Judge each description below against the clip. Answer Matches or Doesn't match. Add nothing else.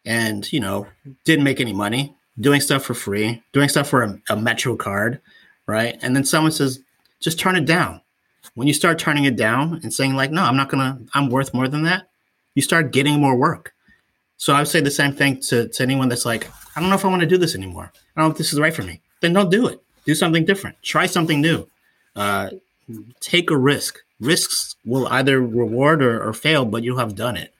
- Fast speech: Matches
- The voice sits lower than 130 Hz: Doesn't match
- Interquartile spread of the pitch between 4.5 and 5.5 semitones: Matches